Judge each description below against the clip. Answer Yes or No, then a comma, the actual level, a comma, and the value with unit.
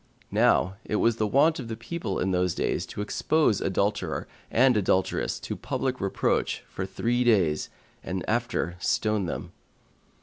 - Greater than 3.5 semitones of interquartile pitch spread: Yes, average, 4.4 semitones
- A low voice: Yes, low, 110 Hz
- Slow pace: No, average, 155 wpm